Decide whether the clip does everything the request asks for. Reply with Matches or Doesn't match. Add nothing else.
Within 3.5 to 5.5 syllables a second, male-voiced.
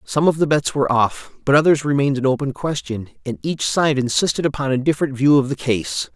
Doesn't match